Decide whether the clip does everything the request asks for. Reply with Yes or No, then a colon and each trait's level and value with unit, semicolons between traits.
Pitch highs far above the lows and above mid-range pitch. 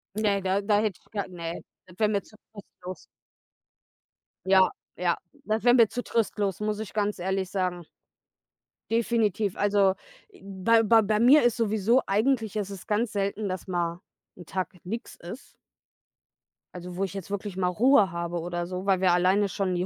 No: average, 2.9 semitones; high, 200 Hz